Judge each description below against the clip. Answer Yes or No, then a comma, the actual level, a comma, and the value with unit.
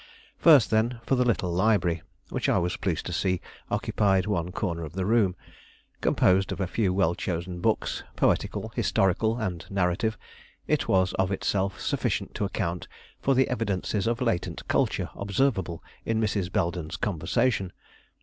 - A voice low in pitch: Yes, very low, 95 Hz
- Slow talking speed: No, average, 155 wpm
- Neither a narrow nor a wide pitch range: Yes, average, 3.7 semitones